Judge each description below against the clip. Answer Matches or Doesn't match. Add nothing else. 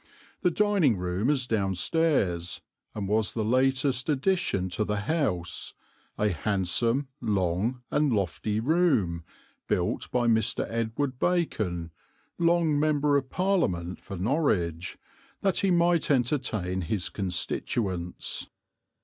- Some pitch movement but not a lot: Doesn't match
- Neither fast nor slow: Doesn't match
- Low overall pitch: Matches